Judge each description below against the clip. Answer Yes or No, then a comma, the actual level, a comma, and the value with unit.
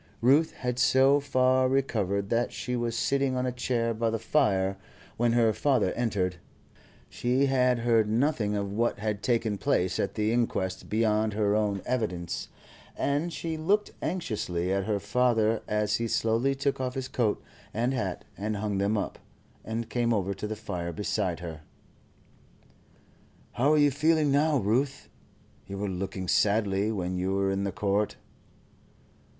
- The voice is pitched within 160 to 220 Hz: No, low, 110 Hz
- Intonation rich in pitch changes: No, average, 4.1 semitones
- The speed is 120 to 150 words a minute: No, average, 160 wpm